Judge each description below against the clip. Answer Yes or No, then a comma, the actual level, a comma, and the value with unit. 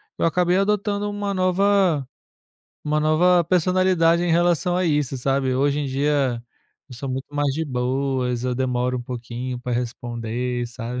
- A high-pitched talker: No, medium, 140 Hz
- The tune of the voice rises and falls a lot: Yes, wide, 5.8 semitones